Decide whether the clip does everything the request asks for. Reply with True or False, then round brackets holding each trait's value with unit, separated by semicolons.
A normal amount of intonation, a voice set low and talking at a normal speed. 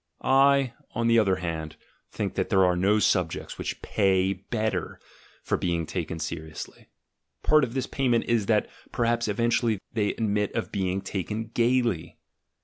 True (4.2 semitones; 105 Hz; 150 wpm)